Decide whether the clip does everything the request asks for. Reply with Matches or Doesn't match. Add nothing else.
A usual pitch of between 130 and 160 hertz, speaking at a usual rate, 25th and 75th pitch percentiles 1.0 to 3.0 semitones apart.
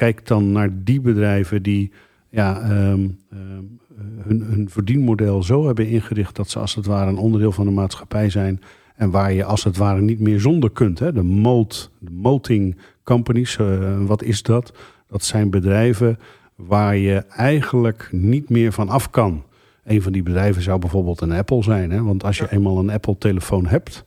Doesn't match